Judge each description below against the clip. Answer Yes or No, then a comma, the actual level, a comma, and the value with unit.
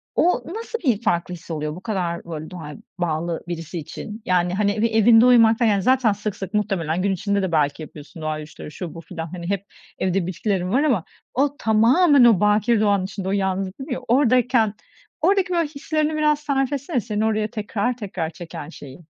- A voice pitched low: No, high, 205 Hz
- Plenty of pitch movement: Yes, wide, 5.9 semitones